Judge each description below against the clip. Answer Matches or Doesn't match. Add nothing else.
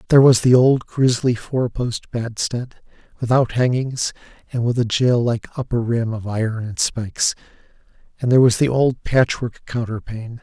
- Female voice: Doesn't match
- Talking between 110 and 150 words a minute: Doesn't match